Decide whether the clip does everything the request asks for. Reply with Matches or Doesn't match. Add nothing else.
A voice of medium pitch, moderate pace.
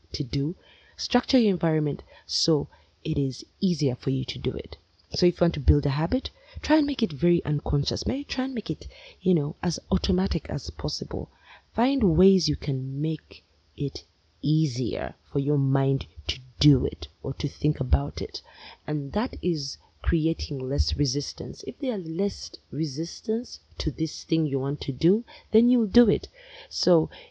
Matches